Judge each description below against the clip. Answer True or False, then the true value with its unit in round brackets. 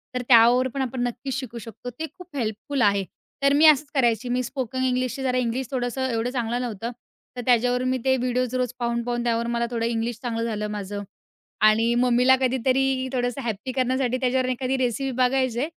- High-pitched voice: True (250 Hz)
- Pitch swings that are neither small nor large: False (1.8 semitones)